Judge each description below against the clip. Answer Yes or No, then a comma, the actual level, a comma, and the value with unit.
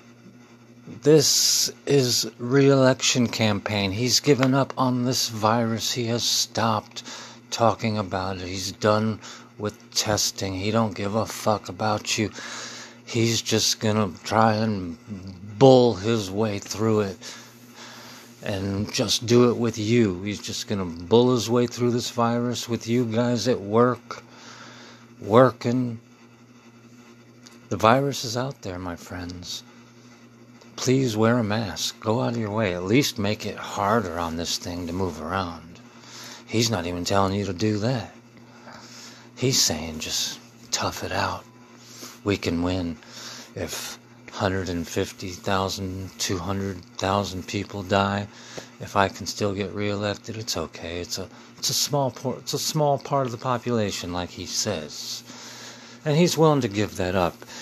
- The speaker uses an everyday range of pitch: Yes, average, 3.2 semitones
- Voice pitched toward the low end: Yes, low, 115 Hz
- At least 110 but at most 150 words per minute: Yes, average, 145 wpm